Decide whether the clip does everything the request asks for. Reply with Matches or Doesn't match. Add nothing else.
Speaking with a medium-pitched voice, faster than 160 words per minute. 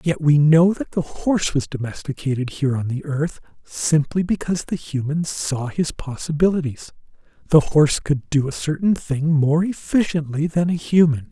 Matches